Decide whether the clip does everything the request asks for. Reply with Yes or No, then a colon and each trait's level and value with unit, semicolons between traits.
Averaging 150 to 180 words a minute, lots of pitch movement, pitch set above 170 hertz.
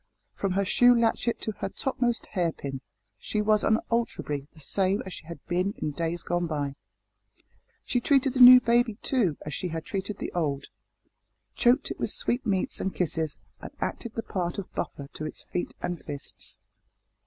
Yes: average, 175 wpm; wide, 6.3 semitones; high, 190 Hz